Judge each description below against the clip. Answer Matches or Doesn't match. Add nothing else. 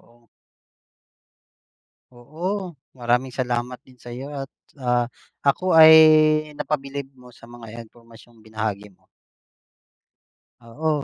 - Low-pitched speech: Matches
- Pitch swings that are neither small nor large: Matches